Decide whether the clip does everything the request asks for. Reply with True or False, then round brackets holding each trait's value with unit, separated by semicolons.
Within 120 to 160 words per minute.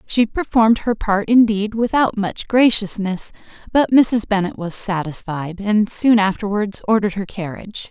True (145 wpm)